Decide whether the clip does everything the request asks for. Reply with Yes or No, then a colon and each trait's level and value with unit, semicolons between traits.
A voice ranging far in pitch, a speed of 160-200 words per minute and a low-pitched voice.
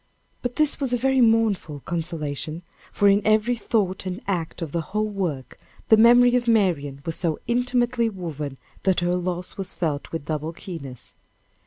No: wide, 5.9 semitones; average, 170 wpm; medium, 185 Hz